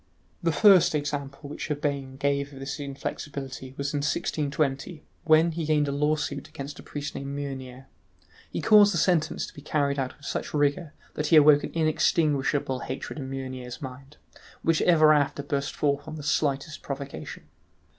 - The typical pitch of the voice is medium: Yes, medium, 145 Hz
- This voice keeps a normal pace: Yes, average, 170 wpm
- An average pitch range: No, narrow, 1.9 semitones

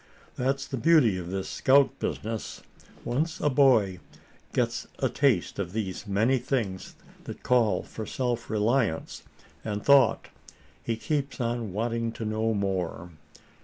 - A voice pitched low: Yes, low, 115 Hz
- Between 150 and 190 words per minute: No, slow, 135 wpm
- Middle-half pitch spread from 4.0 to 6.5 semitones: Yes, average, 4.7 semitones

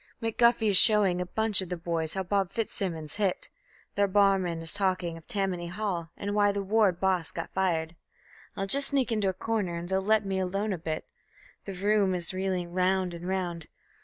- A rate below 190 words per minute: No, average, 195 wpm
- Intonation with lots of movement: No, narrow, 2.6 semitones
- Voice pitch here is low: No, high, 190 Hz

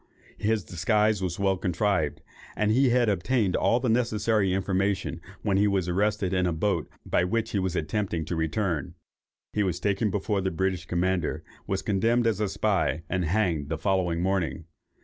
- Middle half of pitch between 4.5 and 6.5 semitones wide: No, average, 3.2 semitones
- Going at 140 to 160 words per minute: No, average, 170 wpm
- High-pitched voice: No, very low, 95 Hz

